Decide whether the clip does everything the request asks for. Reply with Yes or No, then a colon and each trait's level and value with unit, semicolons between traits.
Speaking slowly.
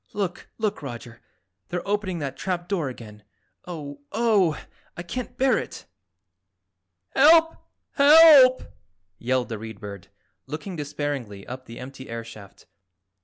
Yes: slow, 125 wpm